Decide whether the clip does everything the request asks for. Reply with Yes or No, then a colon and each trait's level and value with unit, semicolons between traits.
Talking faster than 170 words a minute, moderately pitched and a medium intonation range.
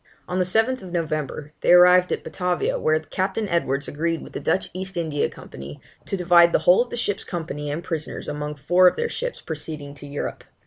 Yes: average, 200 wpm; medium, 170 Hz; average, 3.6 semitones